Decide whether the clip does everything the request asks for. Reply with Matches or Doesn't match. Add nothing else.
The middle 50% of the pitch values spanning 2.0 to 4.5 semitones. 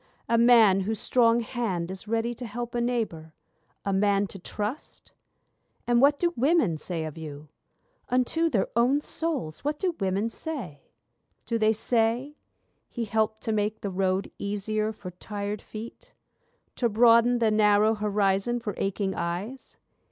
Matches